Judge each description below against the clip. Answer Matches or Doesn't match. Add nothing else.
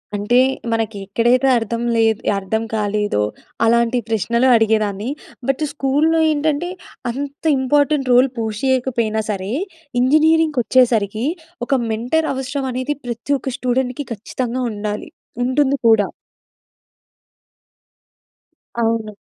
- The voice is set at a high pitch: Matches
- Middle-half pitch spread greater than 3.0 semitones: Matches